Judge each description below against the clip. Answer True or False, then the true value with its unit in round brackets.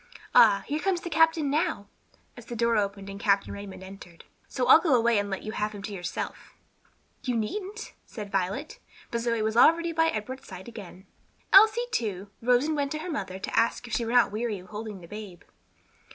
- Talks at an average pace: False (210 wpm)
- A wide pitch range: True (6.1 semitones)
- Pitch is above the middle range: True (230 Hz)